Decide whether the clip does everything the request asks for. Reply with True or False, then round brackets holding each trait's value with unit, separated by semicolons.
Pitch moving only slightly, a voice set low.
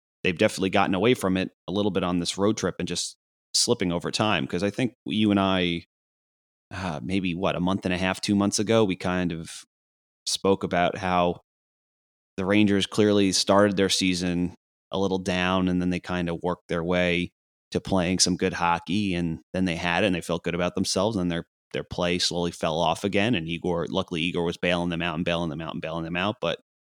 True (2.1 semitones; 90 Hz)